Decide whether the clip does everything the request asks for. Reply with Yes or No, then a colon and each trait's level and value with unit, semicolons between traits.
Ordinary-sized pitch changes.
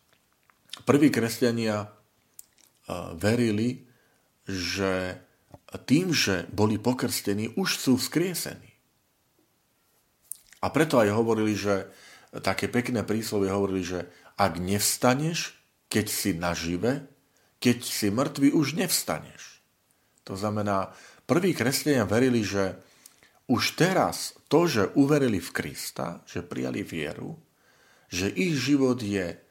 Yes: average, 4.5 semitones